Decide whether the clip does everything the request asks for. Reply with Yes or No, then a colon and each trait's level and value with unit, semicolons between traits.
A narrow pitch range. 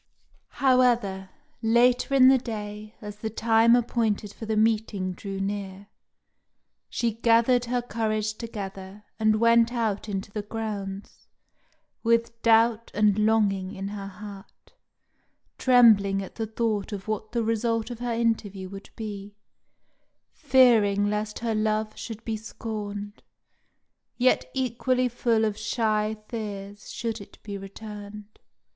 Yes: narrow, 2.2 semitones